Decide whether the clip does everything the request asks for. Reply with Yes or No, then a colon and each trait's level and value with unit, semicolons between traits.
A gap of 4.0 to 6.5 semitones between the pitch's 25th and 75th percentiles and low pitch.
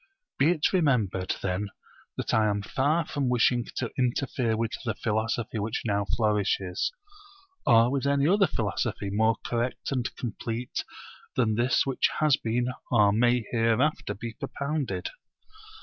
No: average, 3.5 semitones; low, 120 Hz